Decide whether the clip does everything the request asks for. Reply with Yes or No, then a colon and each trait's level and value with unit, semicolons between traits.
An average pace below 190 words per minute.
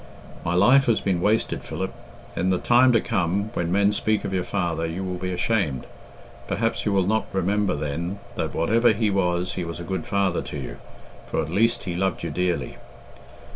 No: average, 200 wpm